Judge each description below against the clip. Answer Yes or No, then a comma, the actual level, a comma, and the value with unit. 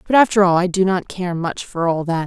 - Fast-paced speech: Yes, fast, 290 wpm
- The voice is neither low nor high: Yes, medium, 180 Hz